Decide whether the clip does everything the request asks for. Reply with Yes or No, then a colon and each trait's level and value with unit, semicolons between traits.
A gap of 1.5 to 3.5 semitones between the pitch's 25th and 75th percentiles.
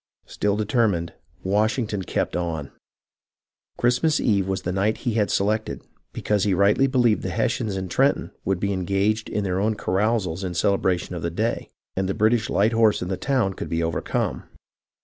Yes: average, 2.9 semitones